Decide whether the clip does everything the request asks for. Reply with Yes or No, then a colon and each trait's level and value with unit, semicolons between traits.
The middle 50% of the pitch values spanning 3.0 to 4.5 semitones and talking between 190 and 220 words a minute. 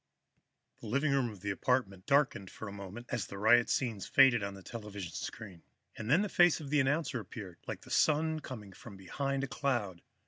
No: wide, 5.6 semitones; fast, 205 wpm